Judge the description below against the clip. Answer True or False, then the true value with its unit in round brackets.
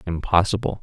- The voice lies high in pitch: False (95 Hz)